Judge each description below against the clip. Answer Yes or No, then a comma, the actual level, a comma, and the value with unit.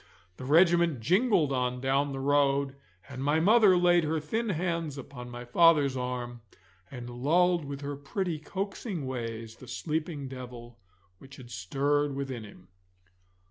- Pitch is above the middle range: No, medium, 140 Hz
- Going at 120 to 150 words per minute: Yes, average, 145 wpm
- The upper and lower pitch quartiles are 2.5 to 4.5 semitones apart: No, average, 4.9 semitones